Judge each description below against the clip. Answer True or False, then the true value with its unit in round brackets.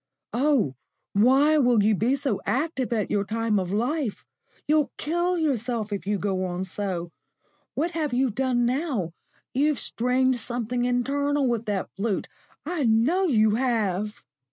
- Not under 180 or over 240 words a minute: False (150 wpm)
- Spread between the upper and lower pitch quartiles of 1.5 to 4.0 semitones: False (5.1 semitones)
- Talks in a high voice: True (245 Hz)